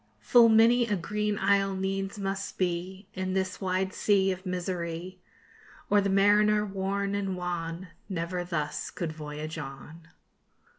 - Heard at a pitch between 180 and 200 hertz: Yes, high, 190 Hz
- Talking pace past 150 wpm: No, average, 140 wpm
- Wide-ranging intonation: No, narrow, 2.4 semitones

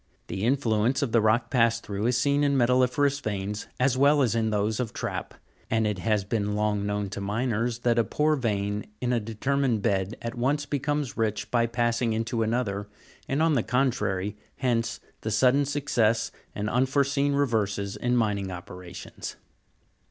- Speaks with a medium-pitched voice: No, low, 115 Hz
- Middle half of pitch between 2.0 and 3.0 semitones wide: No, average, 3.8 semitones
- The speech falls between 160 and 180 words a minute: Yes, average, 175 wpm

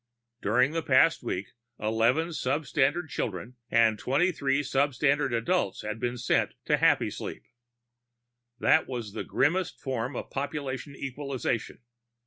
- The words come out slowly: Yes, slow, 125 wpm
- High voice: No, low, 135 Hz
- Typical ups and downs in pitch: Yes, average, 3.9 semitones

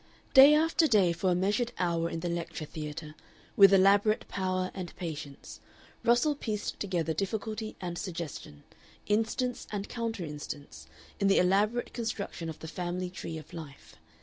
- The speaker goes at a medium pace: Yes, average, 150 wpm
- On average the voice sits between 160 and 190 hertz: Yes, medium, 185 Hz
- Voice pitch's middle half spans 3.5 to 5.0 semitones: Yes, average, 4.4 semitones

